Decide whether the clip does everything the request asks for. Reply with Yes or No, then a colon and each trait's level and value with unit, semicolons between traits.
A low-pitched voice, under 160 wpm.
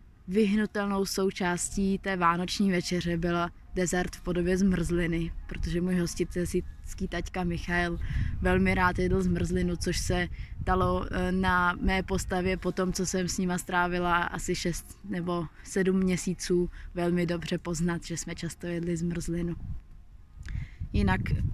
No: medium, 175 Hz; average, 130 wpm